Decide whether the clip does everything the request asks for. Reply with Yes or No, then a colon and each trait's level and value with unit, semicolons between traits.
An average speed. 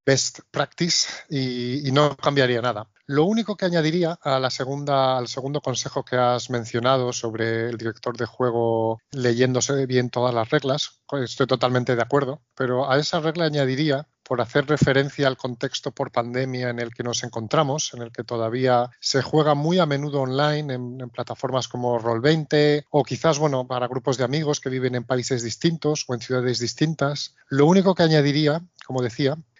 Yes: average, 180 wpm